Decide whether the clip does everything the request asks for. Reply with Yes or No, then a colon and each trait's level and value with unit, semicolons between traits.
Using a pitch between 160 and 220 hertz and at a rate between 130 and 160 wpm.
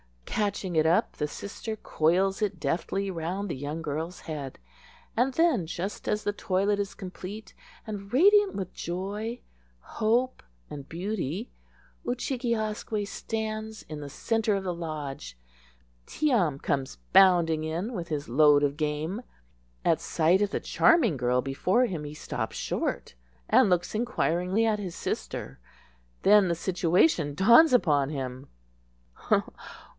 Yes: medium, 185 Hz; average, 145 wpm